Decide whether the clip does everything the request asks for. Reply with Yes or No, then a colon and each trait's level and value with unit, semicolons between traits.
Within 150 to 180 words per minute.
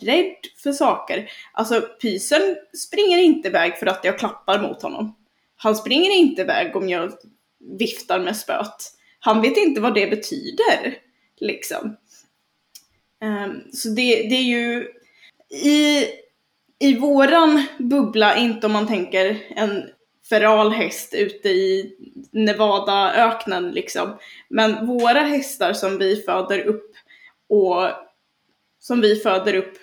No: slow, 125 wpm